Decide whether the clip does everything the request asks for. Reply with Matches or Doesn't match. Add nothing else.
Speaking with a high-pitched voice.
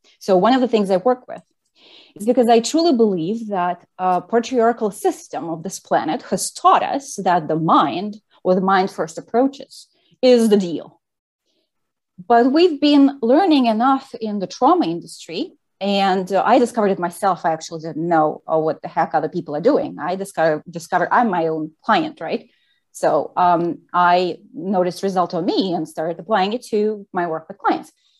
Matches